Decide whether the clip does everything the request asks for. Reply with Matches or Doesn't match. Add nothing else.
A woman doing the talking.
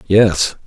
Doesn't match